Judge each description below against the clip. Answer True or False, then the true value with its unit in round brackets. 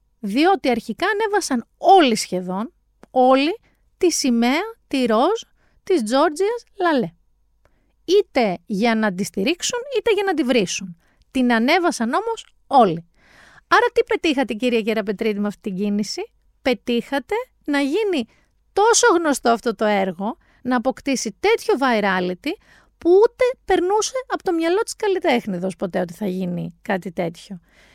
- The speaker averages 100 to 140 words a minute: True (135 wpm)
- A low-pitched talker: False (260 Hz)